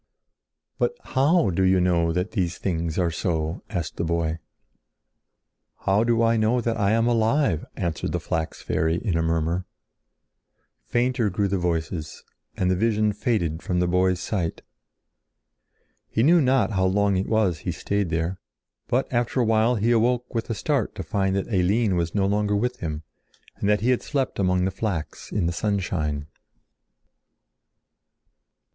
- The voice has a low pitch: Yes, very low, 95 Hz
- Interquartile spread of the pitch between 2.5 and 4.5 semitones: No, average, 4.9 semitones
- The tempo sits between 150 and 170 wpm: Yes, average, 165 wpm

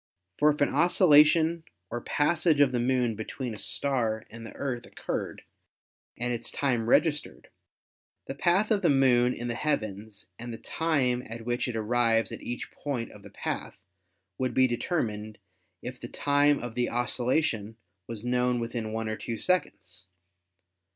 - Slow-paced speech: No, average, 165 wpm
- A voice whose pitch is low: Yes, low, 120 Hz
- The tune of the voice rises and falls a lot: No, average, 4.1 semitones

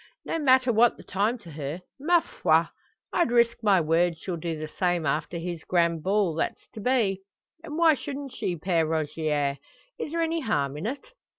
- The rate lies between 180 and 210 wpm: Yes, average, 190 wpm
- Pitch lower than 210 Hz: Yes, medium, 185 Hz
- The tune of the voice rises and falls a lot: Yes, wide, 7.8 semitones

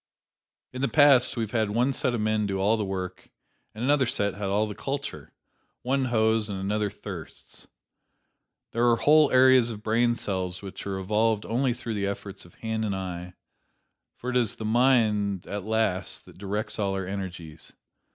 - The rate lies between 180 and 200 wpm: Yes, average, 185 wpm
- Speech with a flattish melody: No, average, 3.4 semitones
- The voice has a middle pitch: No, low, 110 Hz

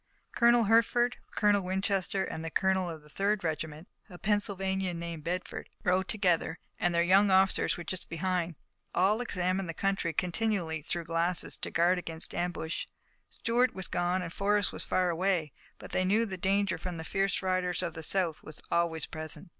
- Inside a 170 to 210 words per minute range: Yes, average, 180 wpm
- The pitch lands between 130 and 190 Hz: Yes, medium, 185 Hz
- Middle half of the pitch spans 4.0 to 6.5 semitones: No, narrow, 2.6 semitones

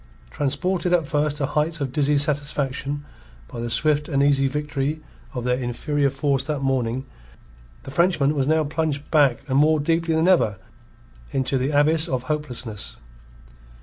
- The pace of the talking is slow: No, average, 155 wpm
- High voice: No, medium, 145 Hz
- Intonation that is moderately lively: No, narrow, 2.3 semitones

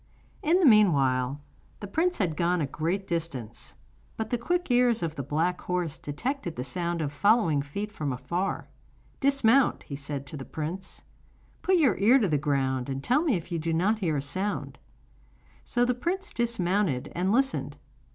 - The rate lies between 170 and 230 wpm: Yes, average, 180 wpm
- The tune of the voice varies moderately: No, wide, 8.2 semitones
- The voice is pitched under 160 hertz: No, medium, 180 Hz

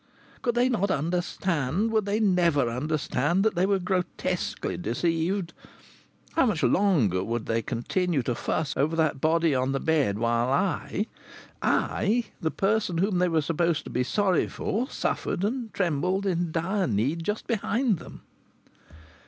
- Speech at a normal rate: Yes, average, 155 wpm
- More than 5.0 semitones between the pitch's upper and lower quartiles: Yes, wide, 5.5 semitones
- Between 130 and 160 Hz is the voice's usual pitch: No, medium, 170 Hz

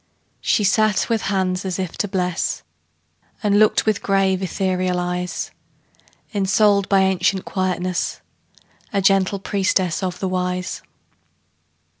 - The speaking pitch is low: No, high, 190 Hz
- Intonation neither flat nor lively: No, narrow, 1.6 semitones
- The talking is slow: Yes, slow, 120 wpm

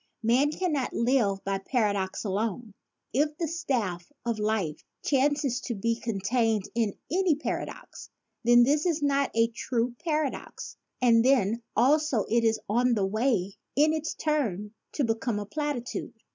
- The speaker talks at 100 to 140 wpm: No, average, 150 wpm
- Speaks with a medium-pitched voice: No, high, 240 Hz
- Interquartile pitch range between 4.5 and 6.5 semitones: Yes, average, 5.1 semitones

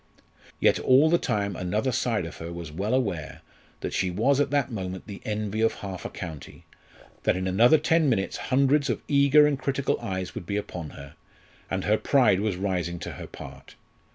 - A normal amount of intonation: No, wide, 6.6 semitones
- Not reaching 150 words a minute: No, average, 195 wpm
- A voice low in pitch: Yes, low, 105 Hz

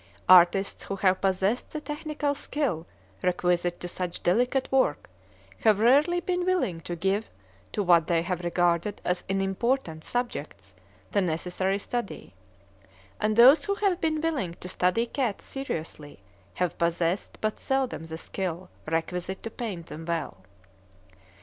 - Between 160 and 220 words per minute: No, average, 140 wpm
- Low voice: No, high, 190 Hz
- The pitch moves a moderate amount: No, wide, 6.4 semitones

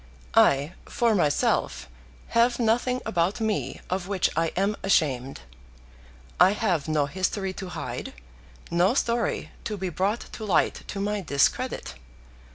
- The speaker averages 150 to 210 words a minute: No, slow, 135 wpm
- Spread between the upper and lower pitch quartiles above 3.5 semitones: Yes, average, 4.5 semitones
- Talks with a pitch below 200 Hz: Yes, high, 190 Hz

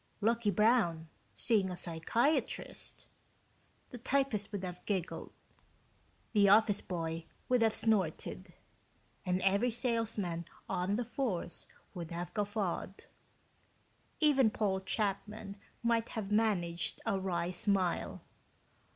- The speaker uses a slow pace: Yes, slow, 110 wpm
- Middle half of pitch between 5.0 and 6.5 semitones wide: No, average, 3.9 semitones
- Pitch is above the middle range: Yes, high, 200 Hz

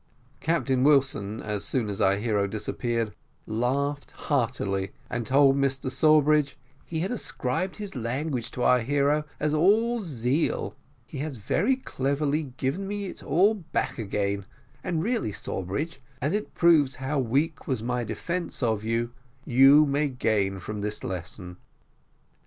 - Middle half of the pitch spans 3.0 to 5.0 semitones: No, wide, 5.5 semitones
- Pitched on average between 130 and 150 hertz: Yes, low, 135 Hz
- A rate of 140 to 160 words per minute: Yes, average, 145 wpm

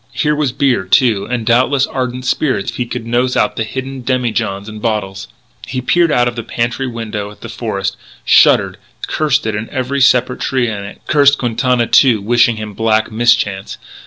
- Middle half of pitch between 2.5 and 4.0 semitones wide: Yes, average, 2.9 semitones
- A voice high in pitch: No, low, 120 Hz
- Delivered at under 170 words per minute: No, average, 190 wpm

